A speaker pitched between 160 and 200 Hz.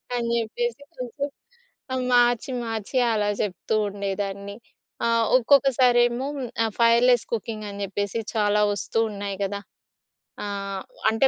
No: high, 225 Hz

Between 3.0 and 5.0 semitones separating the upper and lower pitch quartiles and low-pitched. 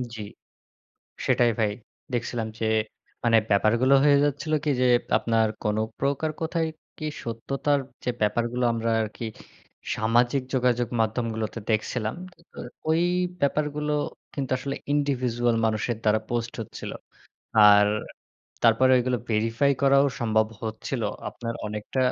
Yes: average, 3.7 semitones; low, 120 Hz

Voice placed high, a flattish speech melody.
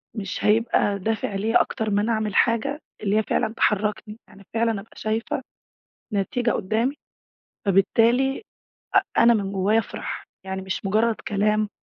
Yes: high, 215 Hz; narrow, 2.3 semitones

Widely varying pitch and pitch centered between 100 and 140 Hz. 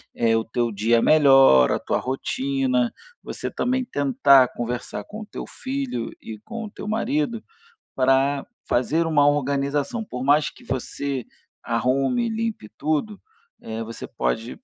Yes: wide, 9.0 semitones; low, 135 Hz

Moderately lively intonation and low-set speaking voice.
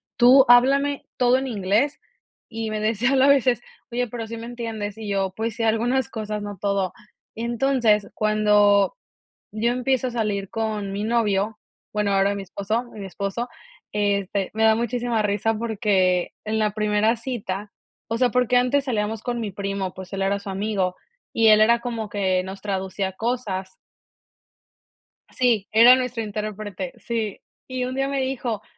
No: average, 3.1 semitones; high, 220 Hz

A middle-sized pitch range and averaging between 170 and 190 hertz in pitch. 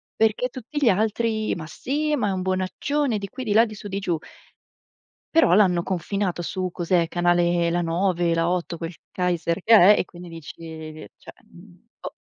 Yes: average, 3.8 semitones; medium, 185 Hz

